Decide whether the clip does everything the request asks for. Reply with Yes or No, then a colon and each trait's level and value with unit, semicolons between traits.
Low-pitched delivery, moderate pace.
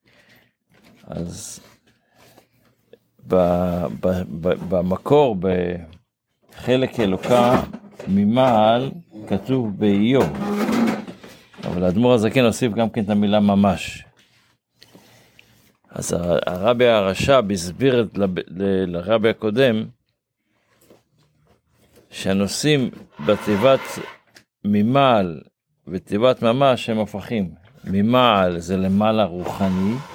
No: low, 110 Hz; slow, 75 wpm